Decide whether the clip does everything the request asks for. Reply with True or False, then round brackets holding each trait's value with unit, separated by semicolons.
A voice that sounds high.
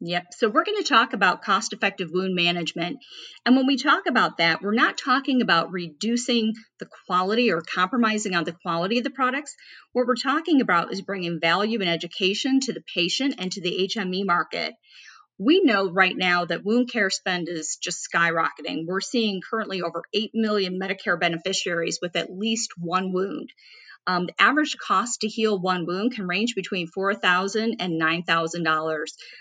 True (195 Hz)